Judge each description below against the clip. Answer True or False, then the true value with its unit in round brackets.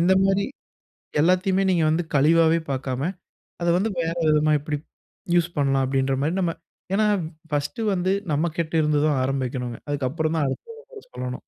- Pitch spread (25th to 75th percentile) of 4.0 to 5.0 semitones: True (4.4 semitones)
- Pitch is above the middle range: False (155 Hz)